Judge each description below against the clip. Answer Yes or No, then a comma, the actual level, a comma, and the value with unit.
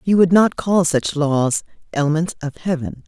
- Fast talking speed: No, average, 175 wpm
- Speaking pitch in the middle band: Yes, medium, 160 Hz